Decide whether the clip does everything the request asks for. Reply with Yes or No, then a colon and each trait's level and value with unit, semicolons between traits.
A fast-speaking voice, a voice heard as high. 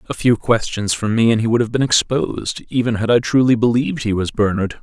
No: fast, 235 wpm; low, 115 Hz